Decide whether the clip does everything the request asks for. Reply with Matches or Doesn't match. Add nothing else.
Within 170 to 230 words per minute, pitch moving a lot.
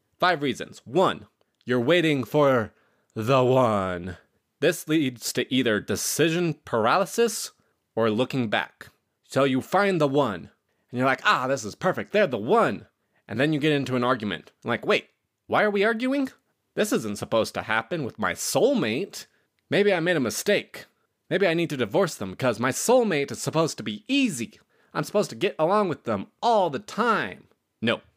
Matches